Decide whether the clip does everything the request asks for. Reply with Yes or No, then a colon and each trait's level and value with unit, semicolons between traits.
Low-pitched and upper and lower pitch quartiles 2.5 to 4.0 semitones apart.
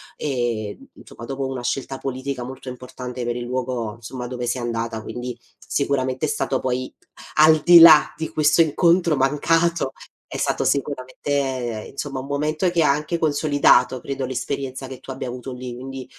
Yes: low, 130 Hz; average, 2.8 semitones